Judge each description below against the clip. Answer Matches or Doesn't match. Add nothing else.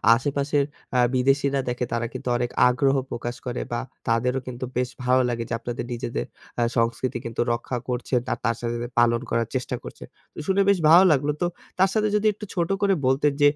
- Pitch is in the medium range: Doesn't match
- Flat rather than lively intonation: Doesn't match